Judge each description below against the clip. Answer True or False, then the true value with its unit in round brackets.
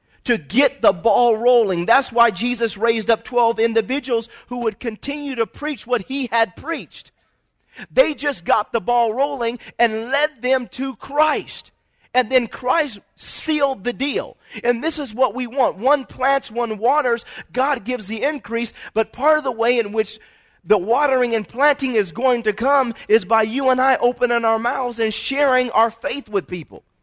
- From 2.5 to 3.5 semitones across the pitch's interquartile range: True (2.8 semitones)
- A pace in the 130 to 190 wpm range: True (180 wpm)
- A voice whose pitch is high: True (245 Hz)